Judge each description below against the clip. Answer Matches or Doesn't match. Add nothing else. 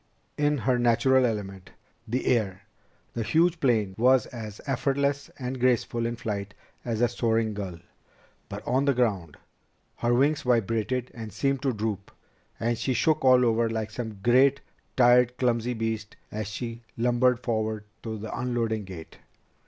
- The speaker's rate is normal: Matches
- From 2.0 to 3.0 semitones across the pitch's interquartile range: Matches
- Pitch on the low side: Matches